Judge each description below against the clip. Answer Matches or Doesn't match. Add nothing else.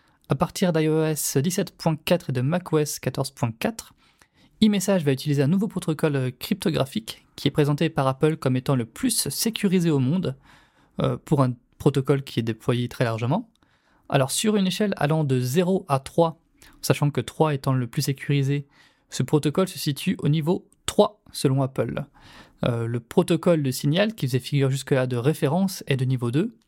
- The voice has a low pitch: Doesn't match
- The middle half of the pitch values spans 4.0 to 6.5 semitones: Matches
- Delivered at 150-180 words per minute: Matches